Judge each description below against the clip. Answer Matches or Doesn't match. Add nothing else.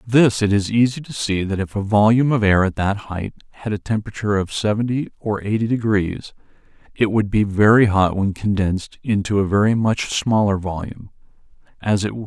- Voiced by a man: Matches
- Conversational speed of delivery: Doesn't match